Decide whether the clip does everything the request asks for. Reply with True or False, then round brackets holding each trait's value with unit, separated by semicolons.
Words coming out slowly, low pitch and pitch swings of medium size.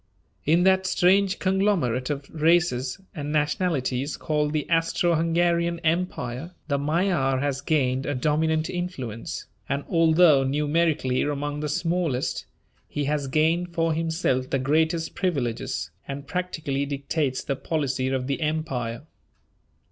False (125 wpm; 150 Hz; 3.6 semitones)